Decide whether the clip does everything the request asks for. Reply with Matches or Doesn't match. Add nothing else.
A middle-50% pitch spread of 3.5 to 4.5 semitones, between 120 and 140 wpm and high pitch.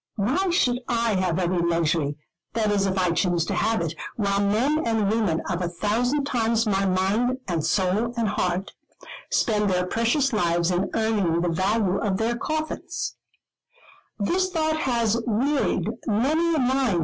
Matches